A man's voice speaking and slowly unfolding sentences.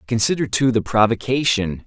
Yes: male; slow, 130 wpm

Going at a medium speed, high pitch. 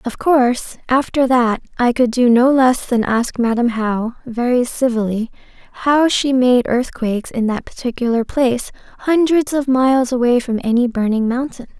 Yes: average, 160 wpm; high, 245 Hz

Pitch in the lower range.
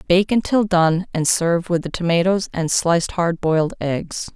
No: medium, 175 Hz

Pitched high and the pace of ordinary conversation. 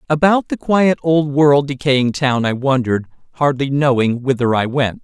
No: medium, 140 Hz; average, 165 wpm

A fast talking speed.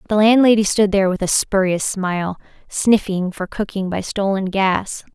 No: average, 165 wpm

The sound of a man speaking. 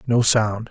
Yes: male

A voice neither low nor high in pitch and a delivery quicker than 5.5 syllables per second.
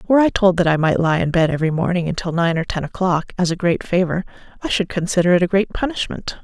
Yes: medium, 180 Hz; 6.6 syllables/s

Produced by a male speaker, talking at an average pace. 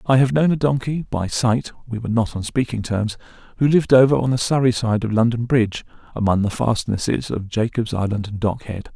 Yes: male; average, 195 wpm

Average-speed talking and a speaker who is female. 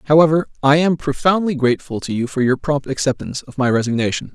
No: average, 195 wpm; male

